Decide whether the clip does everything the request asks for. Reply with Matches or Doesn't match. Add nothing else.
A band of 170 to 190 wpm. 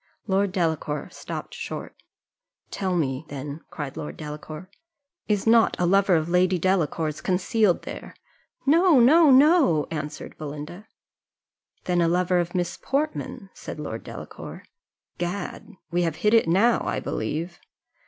Doesn't match